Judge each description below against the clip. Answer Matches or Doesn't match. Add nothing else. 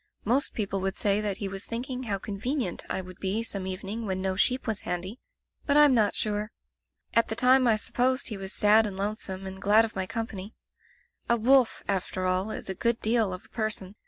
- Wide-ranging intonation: Doesn't match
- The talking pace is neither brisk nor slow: Doesn't match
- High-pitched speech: Matches